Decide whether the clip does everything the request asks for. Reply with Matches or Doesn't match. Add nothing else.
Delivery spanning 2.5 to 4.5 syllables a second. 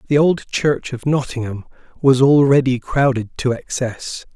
Matches